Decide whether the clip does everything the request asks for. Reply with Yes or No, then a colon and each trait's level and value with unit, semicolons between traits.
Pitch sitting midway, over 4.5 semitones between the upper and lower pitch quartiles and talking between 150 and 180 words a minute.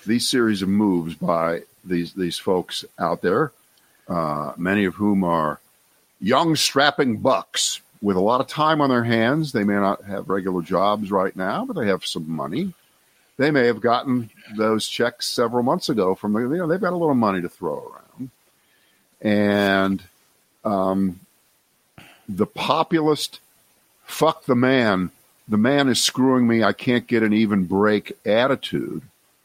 No: low, 110 Hz; average, 5.0 semitones; average, 160 wpm